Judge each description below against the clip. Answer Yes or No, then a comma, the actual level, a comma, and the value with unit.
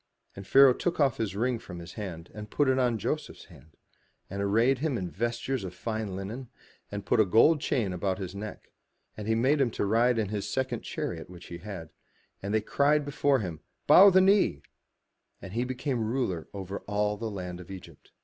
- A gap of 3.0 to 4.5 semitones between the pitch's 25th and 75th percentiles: No, average, 5.1 semitones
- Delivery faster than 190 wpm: Yes, fast, 205 wpm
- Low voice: Yes, low, 110 Hz